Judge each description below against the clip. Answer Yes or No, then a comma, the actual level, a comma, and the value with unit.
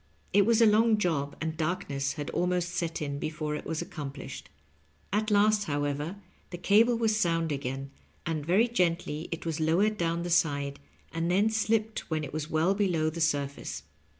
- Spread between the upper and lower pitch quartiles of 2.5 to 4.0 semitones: No, average, 5.2 semitones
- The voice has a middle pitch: Yes, medium, 165 Hz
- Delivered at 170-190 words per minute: Yes, average, 180 wpm